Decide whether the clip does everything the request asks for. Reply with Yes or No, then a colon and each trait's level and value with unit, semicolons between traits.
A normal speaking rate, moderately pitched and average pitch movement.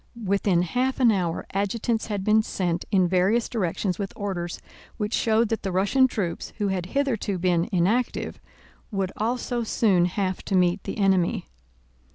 No: average, 160 wpm; high, 200 Hz; average, 3.5 semitones